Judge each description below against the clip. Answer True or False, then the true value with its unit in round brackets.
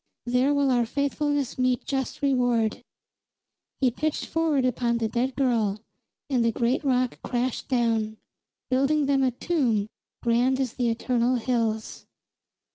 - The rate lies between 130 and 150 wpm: True (135 wpm)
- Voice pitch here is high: True (250 Hz)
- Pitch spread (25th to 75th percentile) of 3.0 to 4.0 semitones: False (2.5 semitones)